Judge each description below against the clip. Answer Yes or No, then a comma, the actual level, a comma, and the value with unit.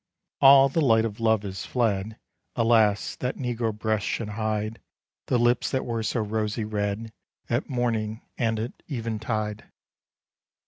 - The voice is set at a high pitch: No, low, 110 Hz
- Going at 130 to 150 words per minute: Yes, average, 145 wpm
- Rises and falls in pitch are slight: Yes, narrow, 2.0 semitones